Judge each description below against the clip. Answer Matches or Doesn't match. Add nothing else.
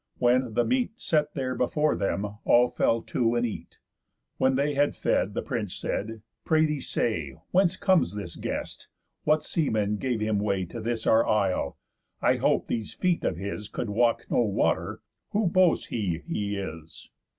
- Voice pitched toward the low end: Matches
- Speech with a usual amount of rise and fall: Doesn't match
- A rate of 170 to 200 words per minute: Matches